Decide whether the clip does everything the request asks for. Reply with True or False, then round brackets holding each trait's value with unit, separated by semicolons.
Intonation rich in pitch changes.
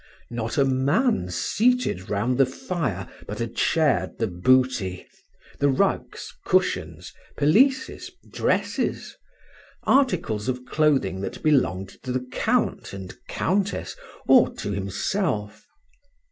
True (7.5 semitones)